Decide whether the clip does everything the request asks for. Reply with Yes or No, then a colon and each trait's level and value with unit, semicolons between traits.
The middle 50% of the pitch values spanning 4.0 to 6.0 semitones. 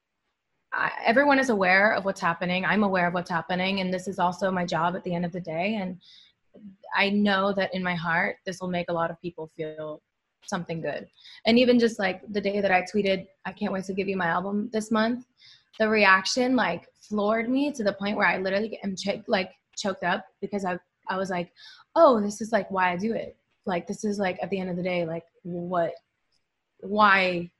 No: narrow, 2.6 semitones